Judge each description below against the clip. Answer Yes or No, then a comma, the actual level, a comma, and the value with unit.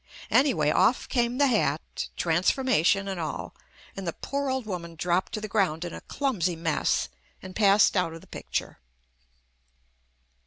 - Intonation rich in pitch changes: Yes, wide, 6.0 semitones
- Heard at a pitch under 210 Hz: Yes, high, 190 Hz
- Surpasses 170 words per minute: No, average, 150 wpm